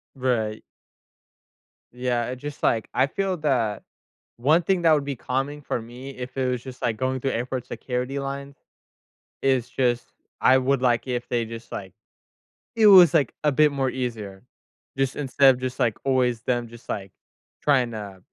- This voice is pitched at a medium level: No, low, 130 Hz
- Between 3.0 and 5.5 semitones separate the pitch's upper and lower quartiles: No, narrow, 2.5 semitones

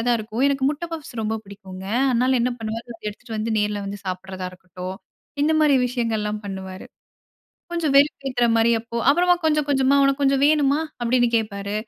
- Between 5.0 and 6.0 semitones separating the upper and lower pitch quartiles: Yes, average, 5.3 semitones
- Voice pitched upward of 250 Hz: No, high, 235 Hz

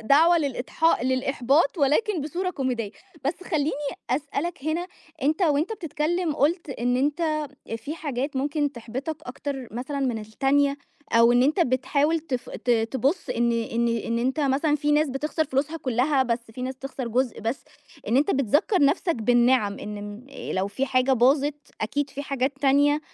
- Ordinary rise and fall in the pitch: Yes, average, 3.6 semitones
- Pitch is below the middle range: No, very high, 275 Hz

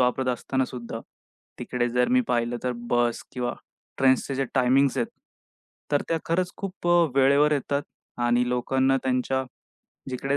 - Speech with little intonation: Yes, narrow, 2.0 semitones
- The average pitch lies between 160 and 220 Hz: No, low, 130 Hz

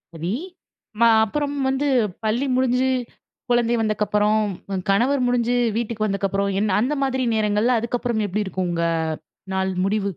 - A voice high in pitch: Yes, high, 220 Hz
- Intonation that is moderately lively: Yes, average, 3.5 semitones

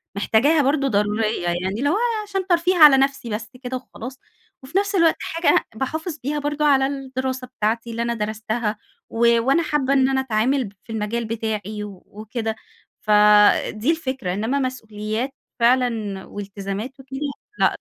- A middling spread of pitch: Yes, average, 4.4 semitones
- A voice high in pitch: Yes, high, 245 Hz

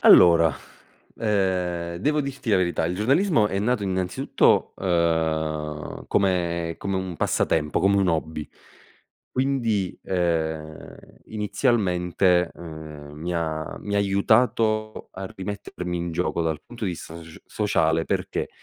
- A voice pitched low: Yes, very low, 90 Hz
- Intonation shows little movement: No, average, 3.9 semitones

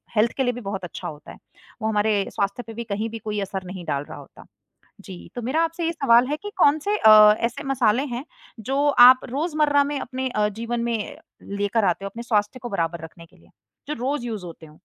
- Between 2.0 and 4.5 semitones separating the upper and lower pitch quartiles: No, average, 5.1 semitones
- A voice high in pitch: Yes, high, 230 Hz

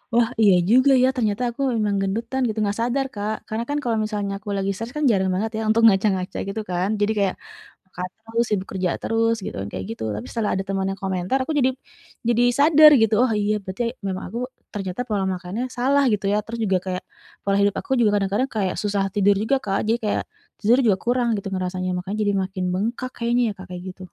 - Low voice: No, high, 205 Hz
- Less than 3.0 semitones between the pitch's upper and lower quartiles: No, average, 3.4 semitones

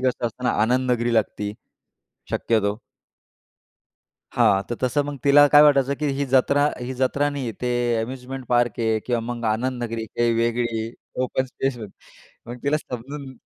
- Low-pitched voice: Yes, low, 125 Hz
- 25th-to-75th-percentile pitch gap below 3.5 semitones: Yes, narrow, 2.6 semitones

